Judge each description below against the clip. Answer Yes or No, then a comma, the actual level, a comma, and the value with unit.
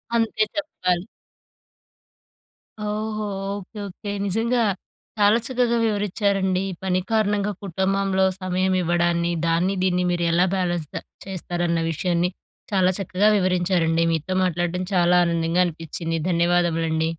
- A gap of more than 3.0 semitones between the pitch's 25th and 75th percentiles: No, narrow, 2.6 semitones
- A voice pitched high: No, medium, 180 Hz